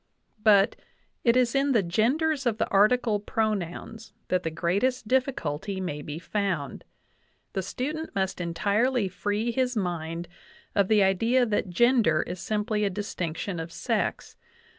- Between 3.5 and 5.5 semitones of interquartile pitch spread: Yes, average, 5.0 semitones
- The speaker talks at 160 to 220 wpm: No, average, 140 wpm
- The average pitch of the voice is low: No, high, 205 Hz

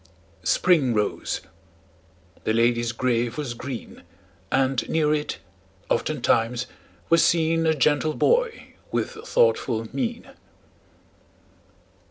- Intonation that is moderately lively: No, wide, 5.8 semitones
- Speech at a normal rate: No, slow, 95 wpm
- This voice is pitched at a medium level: Yes, medium, 145 Hz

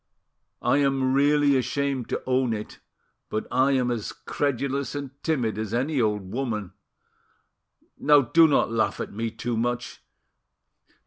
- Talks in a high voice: No, low, 130 Hz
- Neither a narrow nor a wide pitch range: Yes, average, 3.5 semitones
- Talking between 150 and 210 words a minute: No, average, 140 wpm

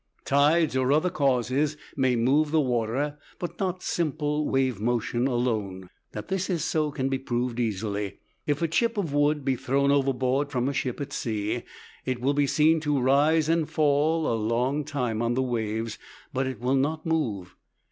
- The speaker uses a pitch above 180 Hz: No, low, 135 Hz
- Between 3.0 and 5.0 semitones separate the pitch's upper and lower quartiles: Yes, average, 3.9 semitones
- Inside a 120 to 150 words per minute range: No, average, 180 wpm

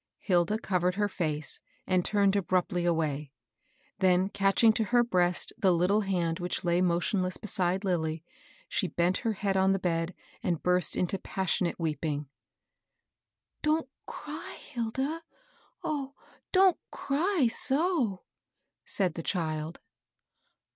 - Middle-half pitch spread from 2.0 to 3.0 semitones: No, average, 4.0 semitones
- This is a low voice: No, medium, 185 Hz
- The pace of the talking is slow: Yes, slow, 130 wpm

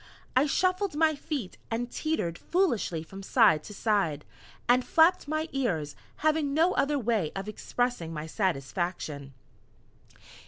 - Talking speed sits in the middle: No, slow, 130 wpm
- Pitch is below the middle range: No, high, 230 Hz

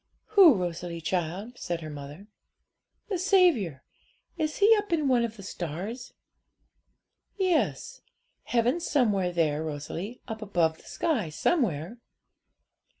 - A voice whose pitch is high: Yes, high, 210 Hz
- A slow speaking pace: Yes, slow, 120 wpm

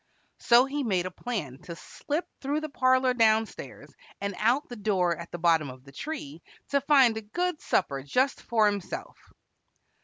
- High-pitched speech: Yes, high, 220 Hz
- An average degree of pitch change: No, wide, 7.4 semitones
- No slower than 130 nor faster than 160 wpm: No, average, 180 wpm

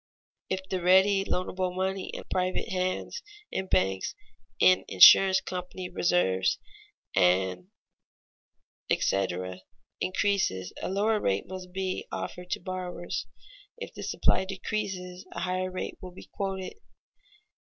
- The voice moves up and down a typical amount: No, narrow, 1.2 semitones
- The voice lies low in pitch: No, medium, 185 Hz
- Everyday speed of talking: No, slow, 115 wpm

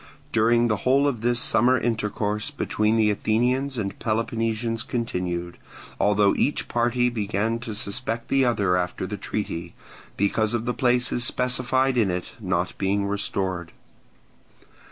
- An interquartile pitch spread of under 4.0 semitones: Yes, average, 3.1 semitones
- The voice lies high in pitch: No, low, 115 Hz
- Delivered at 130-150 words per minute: Yes, average, 140 wpm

